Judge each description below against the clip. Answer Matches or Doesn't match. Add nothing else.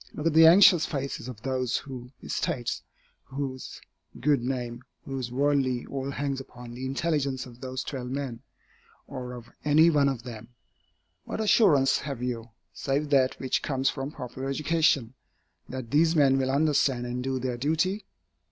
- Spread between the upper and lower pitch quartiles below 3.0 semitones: Matches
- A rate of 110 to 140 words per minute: Doesn't match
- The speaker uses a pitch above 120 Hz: Matches